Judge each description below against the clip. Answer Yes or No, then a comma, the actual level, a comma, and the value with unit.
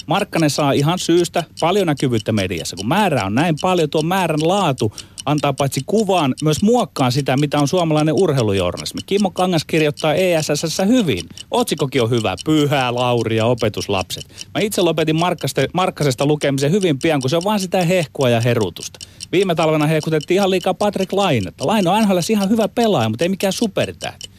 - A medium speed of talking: No, fast, 165 wpm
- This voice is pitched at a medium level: Yes, medium, 155 Hz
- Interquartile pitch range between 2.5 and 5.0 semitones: No, wide, 5.4 semitones